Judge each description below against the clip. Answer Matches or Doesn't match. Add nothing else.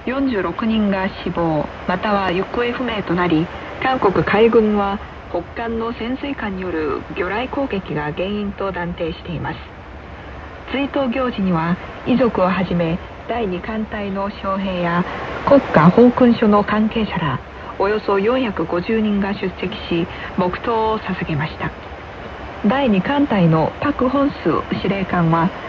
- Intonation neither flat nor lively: Matches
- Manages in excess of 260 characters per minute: Doesn't match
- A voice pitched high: Matches